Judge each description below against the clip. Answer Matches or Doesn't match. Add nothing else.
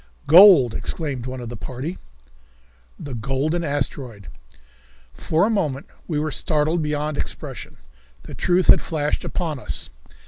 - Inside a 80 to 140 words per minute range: Matches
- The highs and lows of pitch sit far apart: Doesn't match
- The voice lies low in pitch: Doesn't match